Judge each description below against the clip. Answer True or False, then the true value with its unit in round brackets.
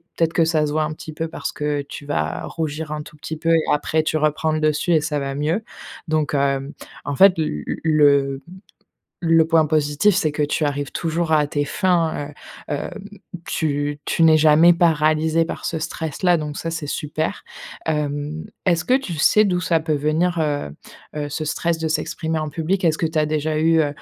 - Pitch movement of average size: False (1.8 semitones)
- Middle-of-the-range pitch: True (155 Hz)